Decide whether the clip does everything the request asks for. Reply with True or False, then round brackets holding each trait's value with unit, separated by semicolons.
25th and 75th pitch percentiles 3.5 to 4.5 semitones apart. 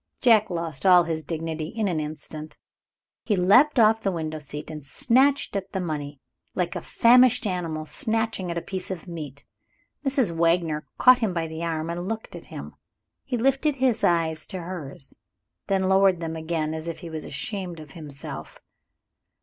False (5.2 semitones)